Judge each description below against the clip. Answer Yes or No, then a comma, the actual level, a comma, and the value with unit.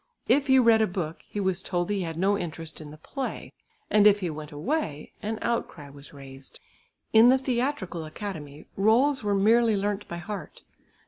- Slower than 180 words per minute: No, average, 185 wpm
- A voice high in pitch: Yes, high, 200 Hz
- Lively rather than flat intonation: Yes, wide, 6.0 semitones